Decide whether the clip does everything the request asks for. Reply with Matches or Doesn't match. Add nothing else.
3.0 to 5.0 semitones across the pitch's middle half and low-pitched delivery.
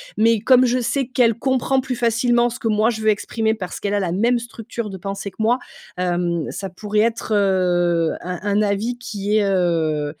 Doesn't match